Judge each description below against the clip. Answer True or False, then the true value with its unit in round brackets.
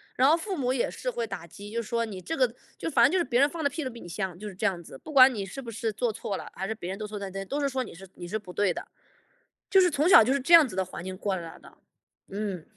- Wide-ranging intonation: True (6.4 semitones)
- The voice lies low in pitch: False (220 Hz)